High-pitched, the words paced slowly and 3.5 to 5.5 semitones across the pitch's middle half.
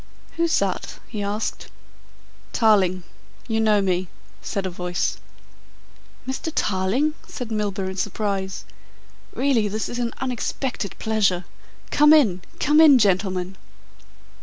Yes: high, 210 Hz; slow, 115 wpm; average, 4.6 semitones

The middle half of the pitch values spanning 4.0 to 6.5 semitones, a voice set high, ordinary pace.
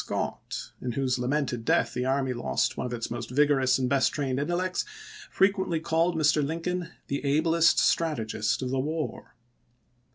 No: average, 4.4 semitones; medium, 140 Hz; average, 165 wpm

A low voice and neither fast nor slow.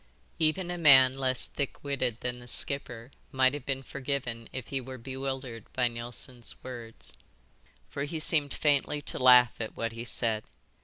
Yes: low, 130 Hz; average, 165 wpm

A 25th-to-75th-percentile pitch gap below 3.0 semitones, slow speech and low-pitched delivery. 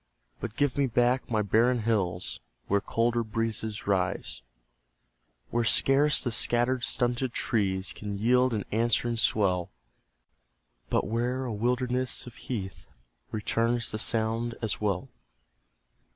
Yes: narrow, 2.5 semitones; slow, 125 wpm; low, 115 Hz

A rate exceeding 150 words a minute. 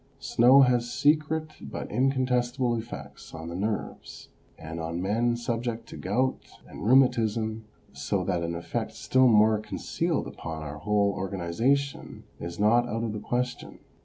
No: average, 145 wpm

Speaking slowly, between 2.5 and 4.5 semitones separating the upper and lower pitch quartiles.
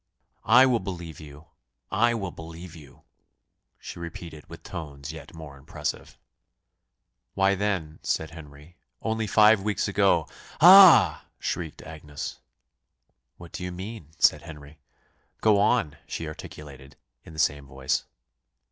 No: slow, 130 wpm; average, 4.9 semitones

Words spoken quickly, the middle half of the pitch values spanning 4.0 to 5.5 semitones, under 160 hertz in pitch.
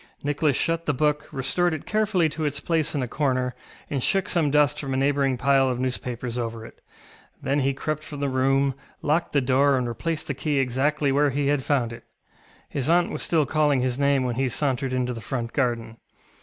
No: fast, 210 wpm; average, 2.7 semitones; medium, 140 Hz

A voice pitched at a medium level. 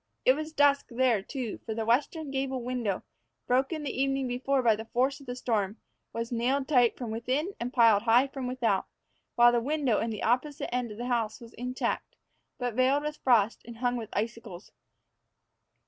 No: high, 245 Hz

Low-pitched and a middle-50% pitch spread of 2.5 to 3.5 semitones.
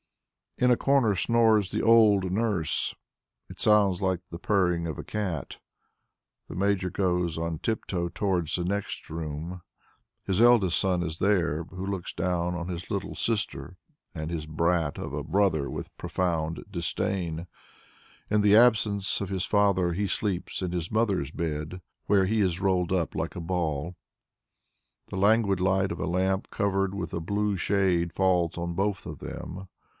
Yes: very low, 95 Hz; average, 3.0 semitones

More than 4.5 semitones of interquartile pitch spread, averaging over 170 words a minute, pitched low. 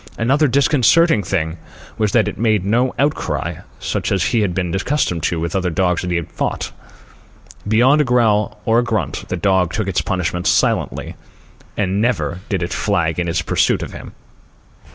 Yes: average, 5.2 semitones; average, 180 wpm; low, 100 Hz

